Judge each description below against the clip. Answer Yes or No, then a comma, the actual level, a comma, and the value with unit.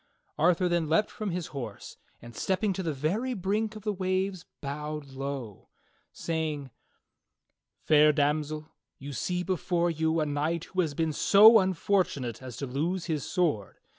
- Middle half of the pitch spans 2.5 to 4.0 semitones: No, average, 4.4 semitones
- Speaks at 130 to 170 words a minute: Yes, average, 160 wpm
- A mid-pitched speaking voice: Yes, medium, 160 Hz